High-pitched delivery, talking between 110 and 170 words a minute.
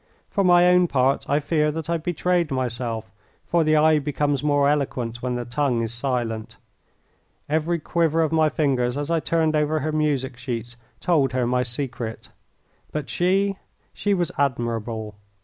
No: medium, 145 Hz; average, 165 wpm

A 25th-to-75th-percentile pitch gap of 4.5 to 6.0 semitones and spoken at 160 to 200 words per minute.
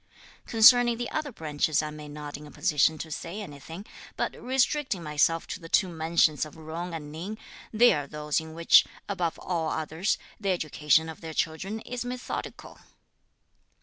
Yes: average, 5.1 semitones; average, 170 wpm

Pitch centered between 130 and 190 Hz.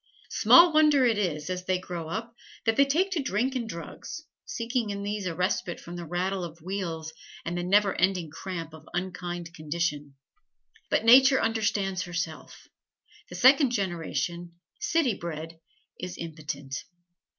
Yes: medium, 185 Hz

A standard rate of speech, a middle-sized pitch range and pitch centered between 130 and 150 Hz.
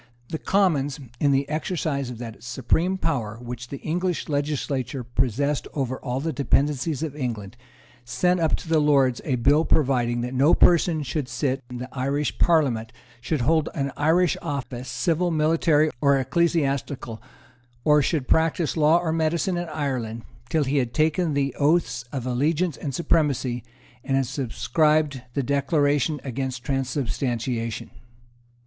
Yes: average, 145 wpm; average, 3.8 semitones; medium, 140 Hz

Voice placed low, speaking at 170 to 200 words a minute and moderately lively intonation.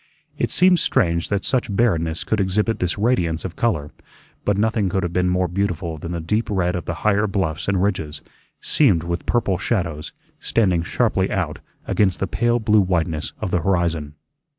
Yes: very low, 90 Hz; average, 180 wpm; average, 4.0 semitones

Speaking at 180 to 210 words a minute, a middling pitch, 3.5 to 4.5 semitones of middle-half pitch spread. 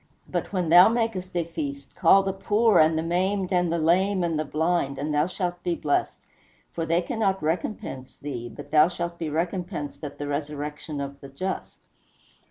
Yes: average, 185 wpm; medium, 170 Hz; average, 3.8 semitones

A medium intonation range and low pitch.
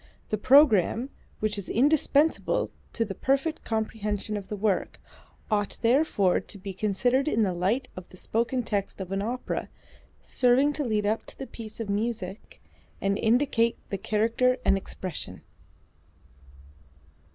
No: average, 4.0 semitones; high, 220 Hz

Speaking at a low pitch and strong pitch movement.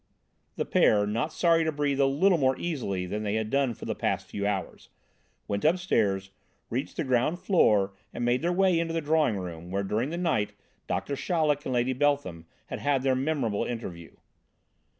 Yes: low, 130 Hz; wide, 7.1 semitones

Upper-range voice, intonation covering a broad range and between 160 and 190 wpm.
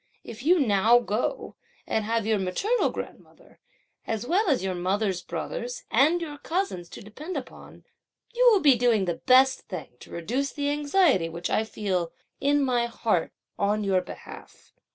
Yes: high, 235 Hz; wide, 6.9 semitones; average, 165 wpm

